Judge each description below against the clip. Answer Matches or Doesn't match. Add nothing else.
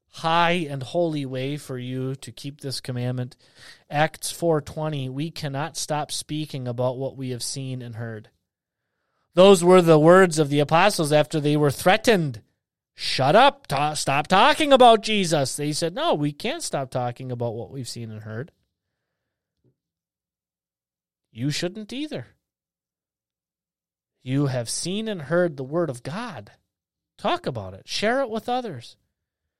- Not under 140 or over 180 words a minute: Matches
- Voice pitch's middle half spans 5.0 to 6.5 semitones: Matches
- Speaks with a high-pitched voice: Doesn't match